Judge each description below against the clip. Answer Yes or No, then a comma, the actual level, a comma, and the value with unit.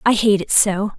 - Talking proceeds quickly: Yes, fast, 245 wpm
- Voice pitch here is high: Yes, high, 200 Hz